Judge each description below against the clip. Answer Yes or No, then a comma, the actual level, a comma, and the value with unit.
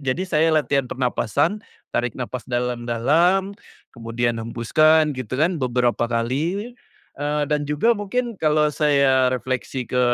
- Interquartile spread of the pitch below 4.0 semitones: No, average, 4.3 semitones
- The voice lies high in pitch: No, medium, 140 Hz